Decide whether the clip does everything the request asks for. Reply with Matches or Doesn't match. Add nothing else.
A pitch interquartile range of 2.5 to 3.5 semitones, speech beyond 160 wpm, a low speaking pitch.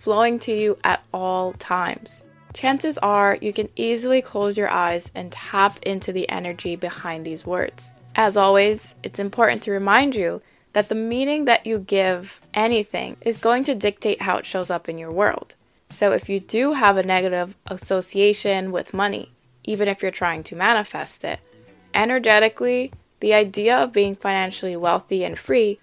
Doesn't match